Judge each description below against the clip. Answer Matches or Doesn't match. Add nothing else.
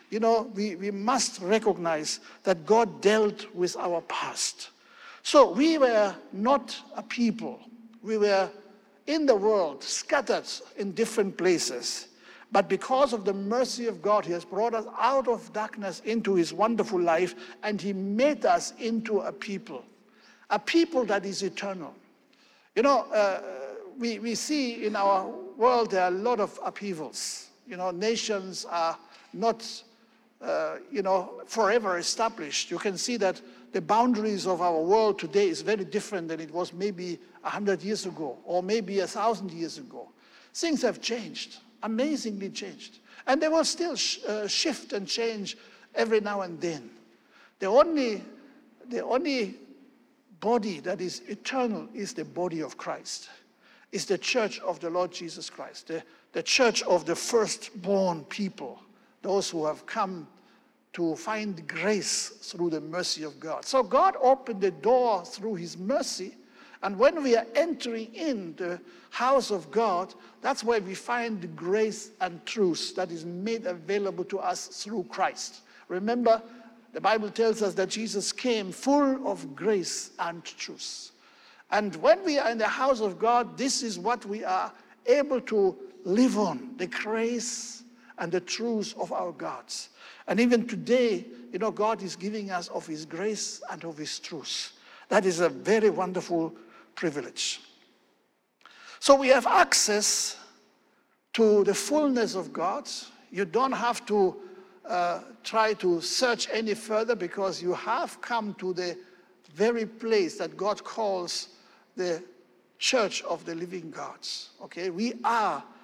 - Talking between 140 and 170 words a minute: Matches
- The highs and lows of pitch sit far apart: Doesn't match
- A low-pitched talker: Doesn't match